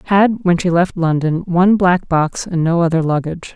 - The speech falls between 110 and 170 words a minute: No, fast, 205 wpm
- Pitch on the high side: No, medium, 175 Hz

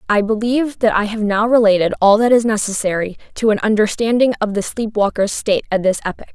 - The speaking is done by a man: No, female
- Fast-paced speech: Yes, fast, 210 wpm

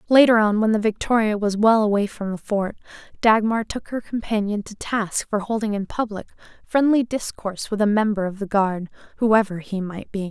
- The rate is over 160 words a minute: Yes, average, 190 wpm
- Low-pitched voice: No, high, 210 Hz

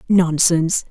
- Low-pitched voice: No, medium, 170 Hz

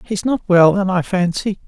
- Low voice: No, high, 190 Hz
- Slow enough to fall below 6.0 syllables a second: Yes, 4.8 syllables/s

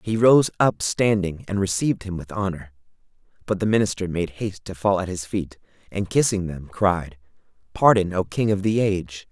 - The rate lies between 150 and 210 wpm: Yes, average, 185 wpm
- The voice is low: Yes, very low, 95 Hz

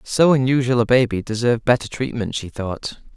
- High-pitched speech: No, low, 120 Hz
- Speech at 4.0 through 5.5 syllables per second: Yes, 5.4 syllables/s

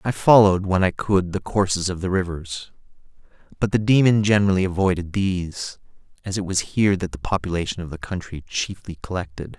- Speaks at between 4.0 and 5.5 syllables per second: No, 5.8 syllables/s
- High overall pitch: No, very low, 95 Hz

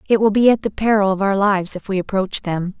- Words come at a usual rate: No, fast, 280 wpm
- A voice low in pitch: No, high, 200 Hz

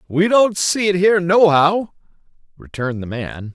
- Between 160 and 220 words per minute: No, average, 150 wpm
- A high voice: No, medium, 170 Hz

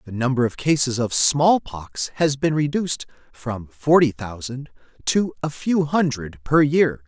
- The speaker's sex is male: Yes, male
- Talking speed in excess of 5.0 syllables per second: No, 4.2 syllables/s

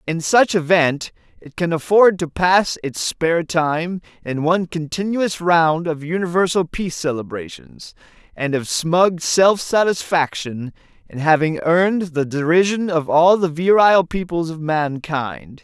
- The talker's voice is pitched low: No, medium, 165 Hz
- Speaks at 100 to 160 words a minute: Yes, average, 140 wpm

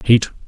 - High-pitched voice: No, low, 115 Hz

